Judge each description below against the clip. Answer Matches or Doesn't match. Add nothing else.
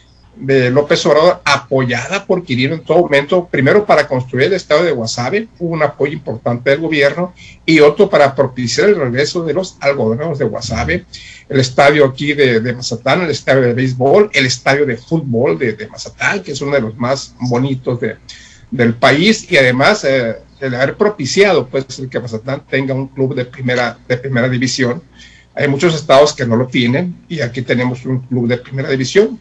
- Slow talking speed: Doesn't match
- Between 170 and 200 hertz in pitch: Doesn't match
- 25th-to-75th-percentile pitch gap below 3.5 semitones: Matches